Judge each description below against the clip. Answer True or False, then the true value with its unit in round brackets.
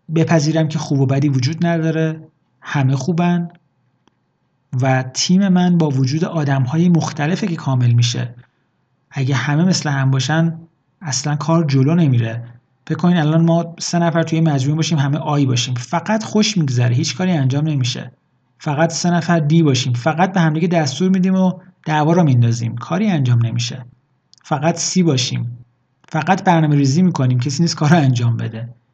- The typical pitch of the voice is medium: True (155 Hz)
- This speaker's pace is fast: True (160 wpm)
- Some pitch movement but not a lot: True (4.2 semitones)